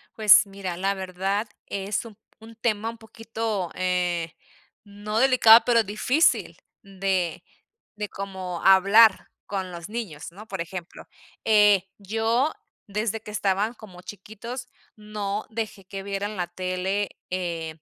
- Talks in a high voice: Yes, high, 200 Hz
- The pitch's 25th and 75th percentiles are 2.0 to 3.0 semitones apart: Yes, average, 2.7 semitones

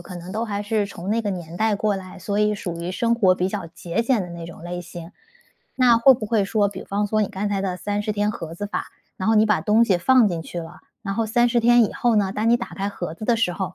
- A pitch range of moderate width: Yes, average, 3.4 semitones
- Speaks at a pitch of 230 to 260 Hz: No, high, 205 Hz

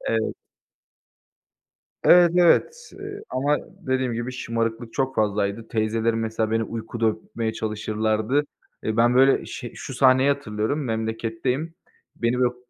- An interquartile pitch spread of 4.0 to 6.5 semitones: No, average, 3.0 semitones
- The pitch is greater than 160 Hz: No, low, 115 Hz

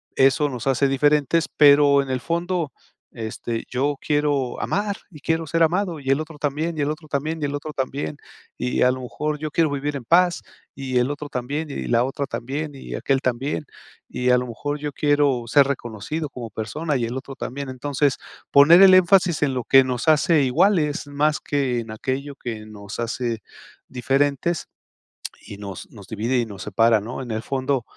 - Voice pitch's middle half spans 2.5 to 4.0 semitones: Yes, average, 3.2 semitones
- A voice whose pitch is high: No, medium, 140 Hz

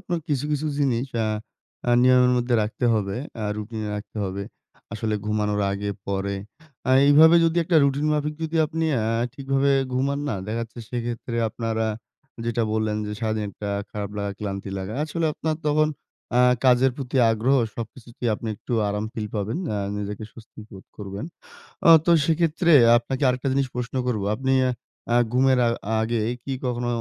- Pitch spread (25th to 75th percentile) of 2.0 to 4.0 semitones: No, average, 4.4 semitones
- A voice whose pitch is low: Yes, low, 120 Hz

